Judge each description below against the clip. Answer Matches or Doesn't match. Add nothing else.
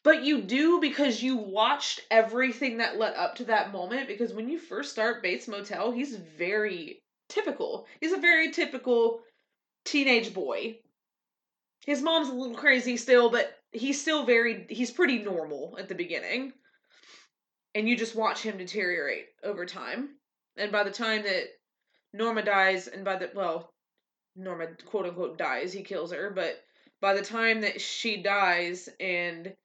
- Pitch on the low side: Doesn't match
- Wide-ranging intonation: Matches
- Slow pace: Doesn't match